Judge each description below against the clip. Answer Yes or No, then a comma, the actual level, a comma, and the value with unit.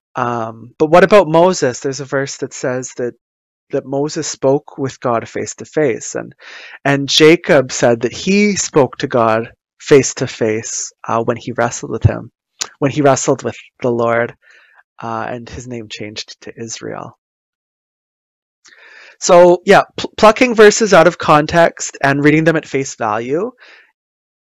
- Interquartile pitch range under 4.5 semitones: No, average, 5.0 semitones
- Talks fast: No, average, 155 wpm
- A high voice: No, low, 135 Hz